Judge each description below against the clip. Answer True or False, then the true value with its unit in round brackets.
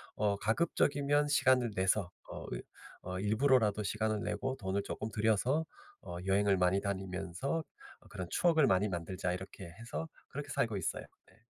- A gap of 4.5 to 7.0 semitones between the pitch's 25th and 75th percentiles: True (5.5 semitones)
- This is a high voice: False (105 Hz)